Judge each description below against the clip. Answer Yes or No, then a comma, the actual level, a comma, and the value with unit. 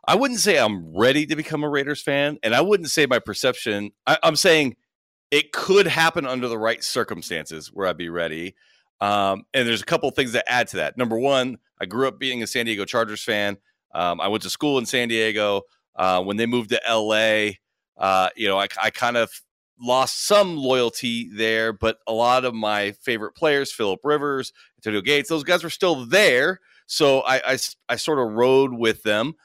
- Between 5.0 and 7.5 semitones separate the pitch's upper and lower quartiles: Yes, wide, 5.5 semitones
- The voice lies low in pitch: Yes, low, 120 Hz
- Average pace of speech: No, fast, 210 wpm